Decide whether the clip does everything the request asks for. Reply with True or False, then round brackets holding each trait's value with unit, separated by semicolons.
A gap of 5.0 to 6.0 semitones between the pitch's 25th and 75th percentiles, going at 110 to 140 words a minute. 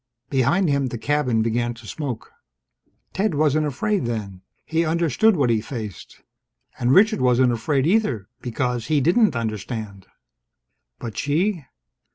True (5.6 semitones; 135 wpm)